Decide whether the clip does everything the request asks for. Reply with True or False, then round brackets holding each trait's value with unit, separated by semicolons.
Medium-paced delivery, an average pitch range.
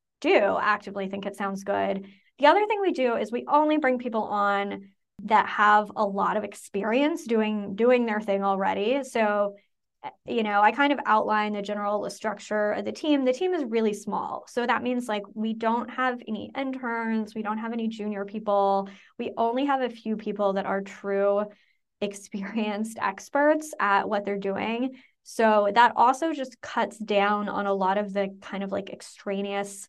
True (185 wpm; 3.1 semitones)